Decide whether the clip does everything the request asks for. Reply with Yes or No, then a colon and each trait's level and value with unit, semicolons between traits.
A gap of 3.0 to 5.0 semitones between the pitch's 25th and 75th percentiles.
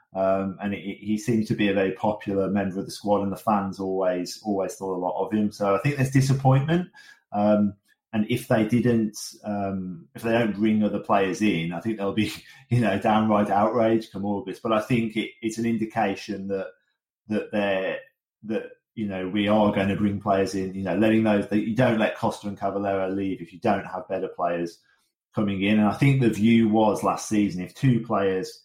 No: narrow, 2.4 semitones